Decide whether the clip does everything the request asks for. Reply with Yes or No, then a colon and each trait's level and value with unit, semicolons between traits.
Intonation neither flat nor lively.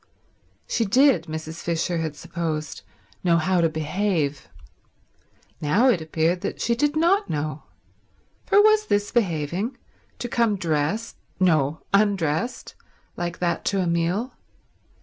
No: wide, 6.1 semitones